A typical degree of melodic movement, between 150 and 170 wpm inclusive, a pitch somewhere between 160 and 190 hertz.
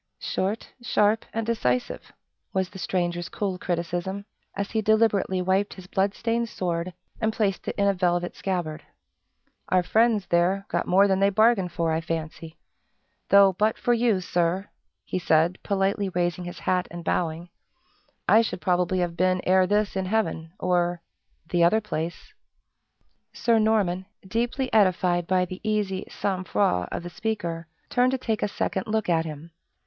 Yes: average, 3.2 semitones; average, 165 wpm; medium, 185 Hz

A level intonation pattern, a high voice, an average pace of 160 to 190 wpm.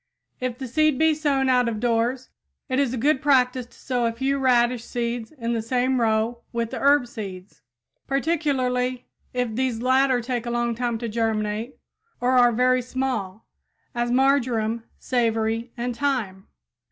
Yes: narrow, 2.1 semitones; high, 245 Hz; average, 165 wpm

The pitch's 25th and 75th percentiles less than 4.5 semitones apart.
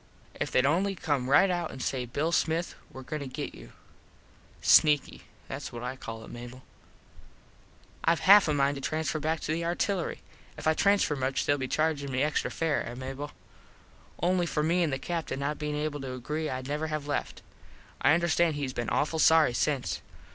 Yes: average, 3.4 semitones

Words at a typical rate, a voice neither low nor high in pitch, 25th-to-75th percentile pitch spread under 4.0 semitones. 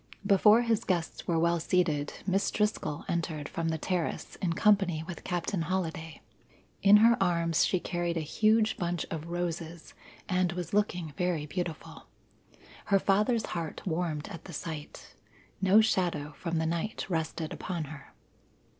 Yes: average, 150 wpm; medium, 175 Hz; average, 2.9 semitones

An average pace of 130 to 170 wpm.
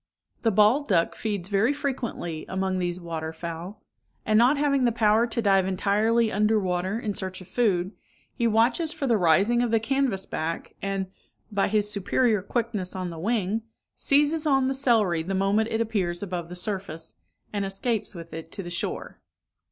No: average, 180 wpm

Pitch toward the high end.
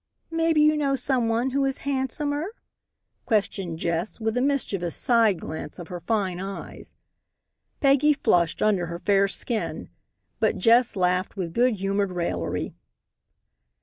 Yes: high, 215 Hz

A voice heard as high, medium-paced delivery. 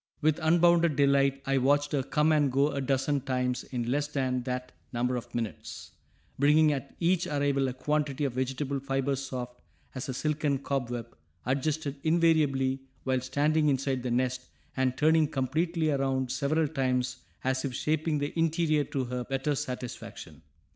No: low, 135 Hz; average, 160 wpm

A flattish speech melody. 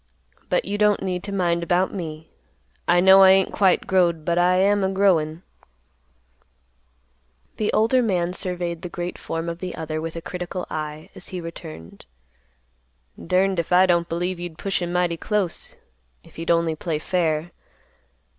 Yes: narrow, 2.2 semitones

